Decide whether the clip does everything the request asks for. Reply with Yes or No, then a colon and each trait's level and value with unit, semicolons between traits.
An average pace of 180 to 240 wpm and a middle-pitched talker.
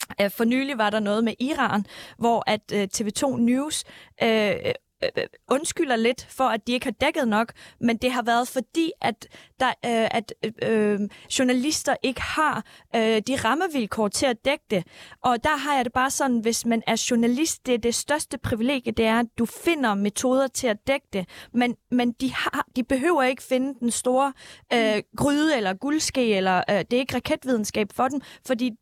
No: average, 190 wpm; very high, 250 Hz